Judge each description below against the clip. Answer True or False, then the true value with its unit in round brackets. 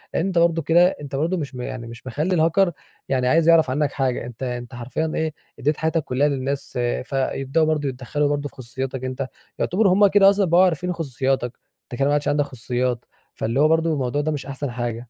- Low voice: False (145 Hz)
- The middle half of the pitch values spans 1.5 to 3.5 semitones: False (4.0 semitones)